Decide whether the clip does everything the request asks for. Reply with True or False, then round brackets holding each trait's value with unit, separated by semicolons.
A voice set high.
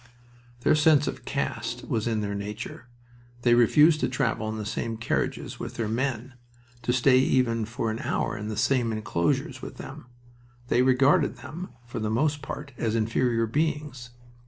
False (120 Hz)